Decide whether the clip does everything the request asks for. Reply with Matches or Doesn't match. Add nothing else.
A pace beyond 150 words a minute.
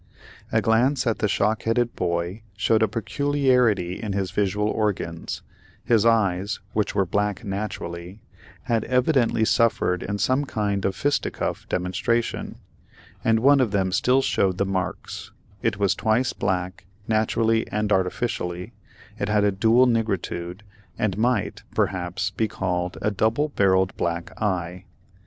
Doesn't match